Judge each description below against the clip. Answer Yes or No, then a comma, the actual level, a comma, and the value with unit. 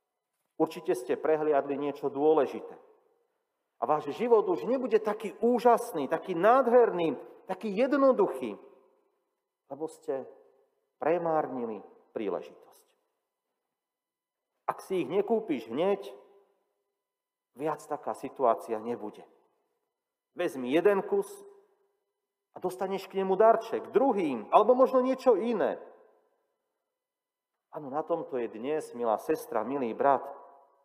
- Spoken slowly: Yes, slow, 100 wpm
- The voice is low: No, very high, 255 Hz